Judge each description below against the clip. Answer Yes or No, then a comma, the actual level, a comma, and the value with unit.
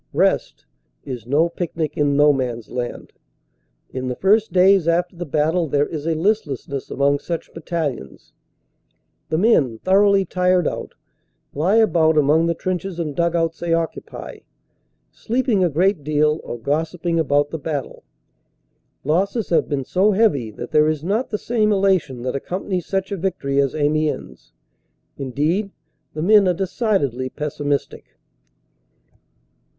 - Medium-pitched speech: Yes, medium, 165 Hz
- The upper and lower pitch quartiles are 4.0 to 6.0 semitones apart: Yes, average, 4.6 semitones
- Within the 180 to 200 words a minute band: No, average, 145 wpm